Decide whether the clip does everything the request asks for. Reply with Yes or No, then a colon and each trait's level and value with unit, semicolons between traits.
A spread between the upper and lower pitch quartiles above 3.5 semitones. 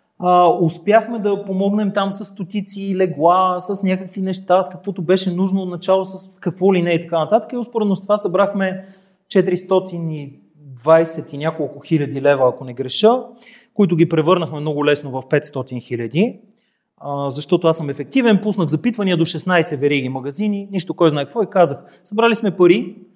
Yes: average, 4.0 semitones